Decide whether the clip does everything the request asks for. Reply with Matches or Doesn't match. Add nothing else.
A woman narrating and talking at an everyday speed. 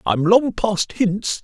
Doesn't match